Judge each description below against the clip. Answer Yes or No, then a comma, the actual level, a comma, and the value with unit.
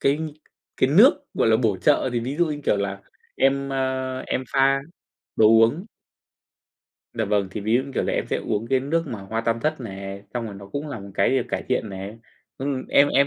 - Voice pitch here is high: No, low, 125 Hz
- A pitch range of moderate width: Yes, average, 4.6 semitones